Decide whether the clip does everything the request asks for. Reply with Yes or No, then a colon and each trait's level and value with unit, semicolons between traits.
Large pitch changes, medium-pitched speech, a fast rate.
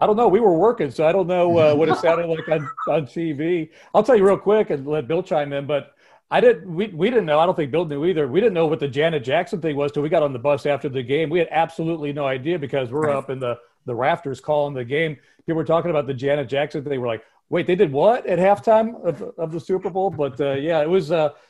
No: average, 3.4 semitones; medium, 160 Hz; fast, 285 wpm